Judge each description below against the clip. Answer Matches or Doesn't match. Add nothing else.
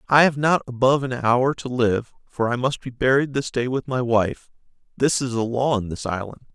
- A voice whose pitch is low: Matches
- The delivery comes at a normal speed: Doesn't match